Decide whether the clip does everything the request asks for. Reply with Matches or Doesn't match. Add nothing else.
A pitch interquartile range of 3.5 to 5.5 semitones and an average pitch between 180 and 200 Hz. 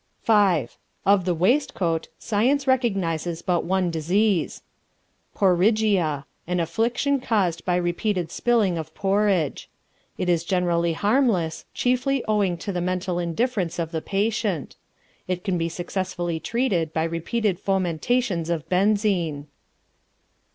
Matches